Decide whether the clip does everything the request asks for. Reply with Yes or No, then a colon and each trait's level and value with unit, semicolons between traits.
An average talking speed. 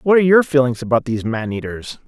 No: fast, 230 wpm